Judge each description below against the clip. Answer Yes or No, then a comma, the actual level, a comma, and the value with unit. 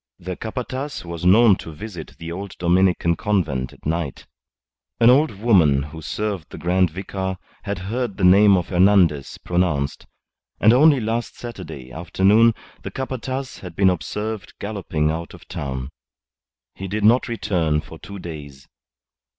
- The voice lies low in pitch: Yes, very low, 95 Hz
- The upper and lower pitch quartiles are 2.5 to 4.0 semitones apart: No, average, 4.8 semitones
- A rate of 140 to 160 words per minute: Yes, average, 150 wpm